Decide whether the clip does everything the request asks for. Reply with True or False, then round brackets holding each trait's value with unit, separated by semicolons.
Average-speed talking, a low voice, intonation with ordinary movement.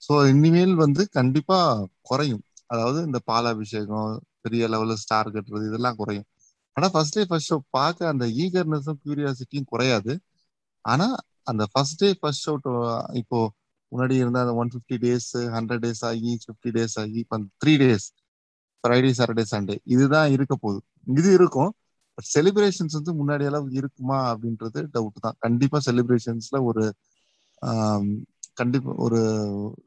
False (135 wpm; 125 Hz; 4.4 semitones)